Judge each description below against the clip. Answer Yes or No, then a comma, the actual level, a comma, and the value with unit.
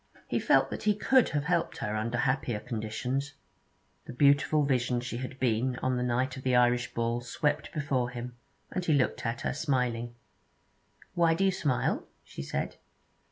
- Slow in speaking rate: No, average, 175 wpm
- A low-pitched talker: Yes, low, 125 Hz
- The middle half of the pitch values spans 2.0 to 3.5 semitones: Yes, average, 3.2 semitones